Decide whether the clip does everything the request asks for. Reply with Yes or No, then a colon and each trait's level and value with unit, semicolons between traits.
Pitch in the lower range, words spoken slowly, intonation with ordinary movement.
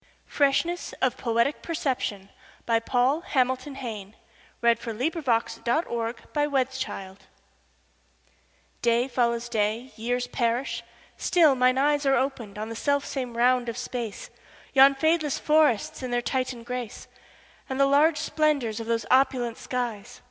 No: very high, 250 Hz; slow, 110 wpm; average, 3.0 semitones